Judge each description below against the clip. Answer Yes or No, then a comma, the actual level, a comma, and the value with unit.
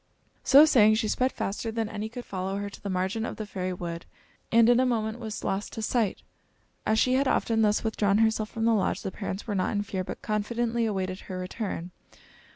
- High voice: Yes, high, 215 Hz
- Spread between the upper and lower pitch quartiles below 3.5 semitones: Yes, average, 2.8 semitones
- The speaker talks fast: Yes, fast, 220 wpm